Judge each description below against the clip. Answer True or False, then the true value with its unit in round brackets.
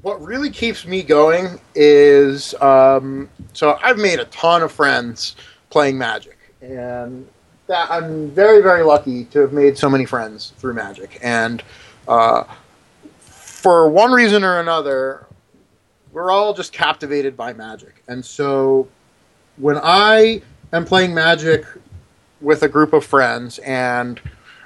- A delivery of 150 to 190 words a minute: False (135 wpm)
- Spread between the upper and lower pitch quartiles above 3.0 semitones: True (4.9 semitones)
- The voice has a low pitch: False (145 Hz)